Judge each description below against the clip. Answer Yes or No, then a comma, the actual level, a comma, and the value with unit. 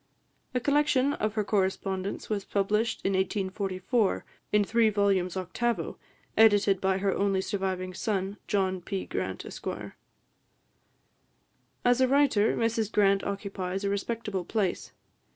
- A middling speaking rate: No, slow, 125 wpm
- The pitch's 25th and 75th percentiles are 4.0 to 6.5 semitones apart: No, narrow, 2.5 semitones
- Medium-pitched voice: No, high, 200 Hz